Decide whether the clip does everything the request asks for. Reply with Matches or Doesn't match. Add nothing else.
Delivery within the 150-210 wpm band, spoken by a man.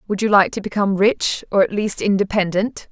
Doesn't match